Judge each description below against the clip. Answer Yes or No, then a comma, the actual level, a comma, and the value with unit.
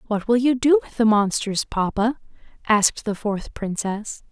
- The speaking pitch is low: No, high, 220 Hz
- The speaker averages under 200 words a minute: Yes, average, 165 wpm